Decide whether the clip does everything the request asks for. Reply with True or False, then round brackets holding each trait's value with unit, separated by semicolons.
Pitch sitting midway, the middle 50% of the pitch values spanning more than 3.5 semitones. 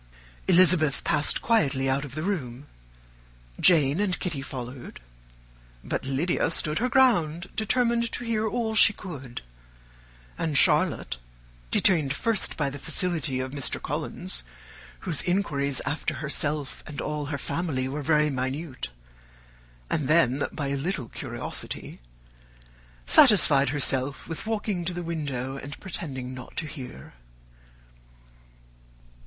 True (150 Hz; 4.9 semitones)